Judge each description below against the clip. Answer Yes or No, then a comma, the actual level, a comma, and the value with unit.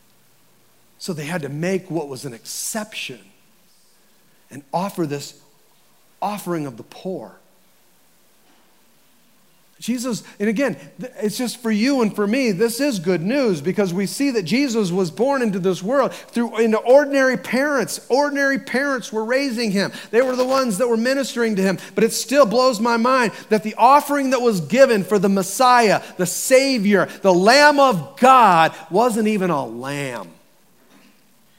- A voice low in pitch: No, high, 220 Hz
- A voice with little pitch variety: No, average, 5.2 semitones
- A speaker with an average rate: Yes, average, 160 wpm